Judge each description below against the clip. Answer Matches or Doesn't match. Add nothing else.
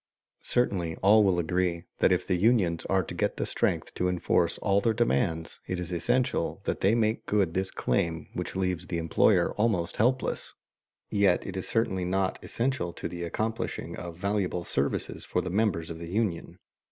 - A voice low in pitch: Matches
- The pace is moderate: Matches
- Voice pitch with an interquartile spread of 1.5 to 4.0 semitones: Matches